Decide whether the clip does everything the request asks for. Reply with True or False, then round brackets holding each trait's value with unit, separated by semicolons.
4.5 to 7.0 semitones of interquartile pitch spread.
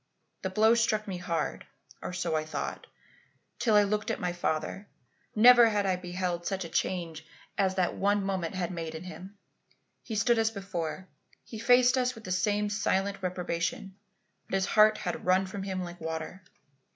False (3.0 semitones)